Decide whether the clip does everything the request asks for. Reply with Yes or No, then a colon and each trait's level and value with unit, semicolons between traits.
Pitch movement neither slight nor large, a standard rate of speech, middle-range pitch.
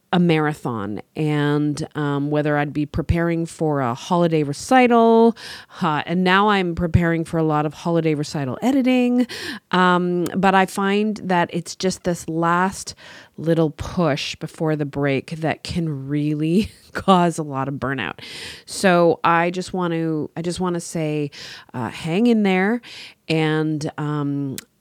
Yes: average, 3.5 semitones; average, 150 wpm; medium, 165 Hz